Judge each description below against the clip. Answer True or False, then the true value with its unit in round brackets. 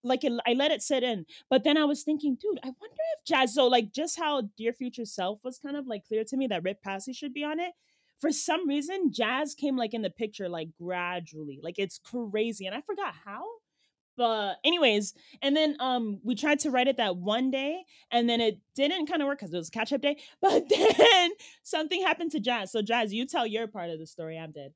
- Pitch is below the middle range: False (255 Hz)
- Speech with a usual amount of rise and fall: False (5.8 semitones)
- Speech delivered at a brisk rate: True (240 wpm)